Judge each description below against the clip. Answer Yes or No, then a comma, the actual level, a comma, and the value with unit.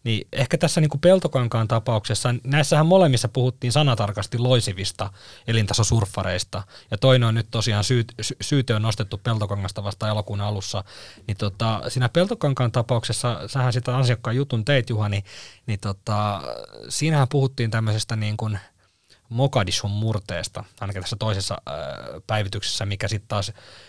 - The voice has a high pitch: No, low, 110 Hz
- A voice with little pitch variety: No, average, 3.3 semitones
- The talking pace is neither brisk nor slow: Yes, average, 135 wpm